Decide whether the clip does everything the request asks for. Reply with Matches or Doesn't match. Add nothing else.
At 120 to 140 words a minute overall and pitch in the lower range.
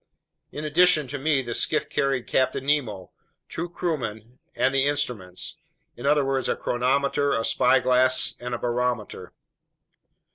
Matches